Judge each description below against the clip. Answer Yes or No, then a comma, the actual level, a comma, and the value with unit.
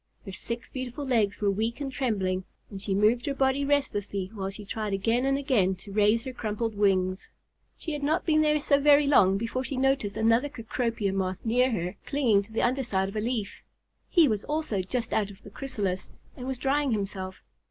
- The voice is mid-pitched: No, high, 225 Hz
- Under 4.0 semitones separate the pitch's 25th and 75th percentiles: No, average, 5.2 semitones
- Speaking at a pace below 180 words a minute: No, fast, 205 wpm